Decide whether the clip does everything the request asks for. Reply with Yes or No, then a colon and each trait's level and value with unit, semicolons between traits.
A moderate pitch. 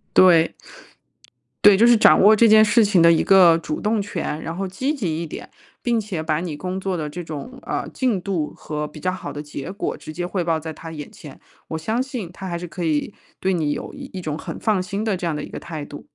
Yes: medium, 180 Hz